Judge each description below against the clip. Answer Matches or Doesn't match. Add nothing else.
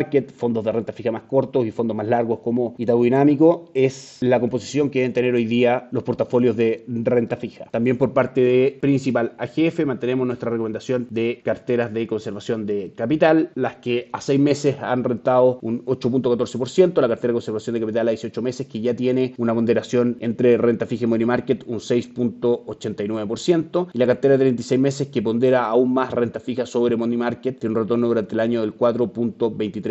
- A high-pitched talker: Doesn't match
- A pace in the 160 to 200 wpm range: Matches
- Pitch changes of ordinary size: Doesn't match